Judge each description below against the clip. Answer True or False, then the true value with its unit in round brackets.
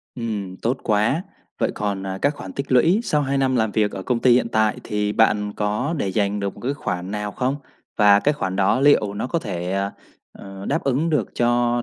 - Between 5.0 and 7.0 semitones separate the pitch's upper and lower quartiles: False (4.4 semitones)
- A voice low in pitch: True (110 Hz)